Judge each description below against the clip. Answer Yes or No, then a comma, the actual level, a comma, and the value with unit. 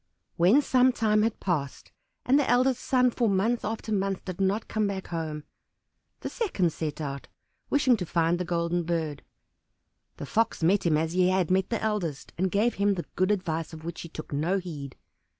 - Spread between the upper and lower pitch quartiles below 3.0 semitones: No, average, 4.8 semitones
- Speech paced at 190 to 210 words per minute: Yes, average, 195 wpm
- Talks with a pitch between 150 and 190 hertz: Yes, medium, 185 Hz